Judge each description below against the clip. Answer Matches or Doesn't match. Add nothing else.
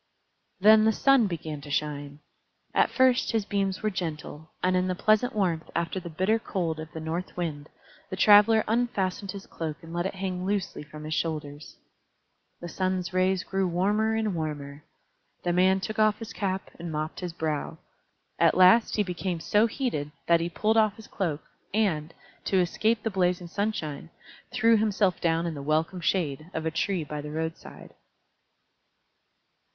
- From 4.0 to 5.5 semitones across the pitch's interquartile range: Matches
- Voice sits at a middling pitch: Matches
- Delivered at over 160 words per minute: Matches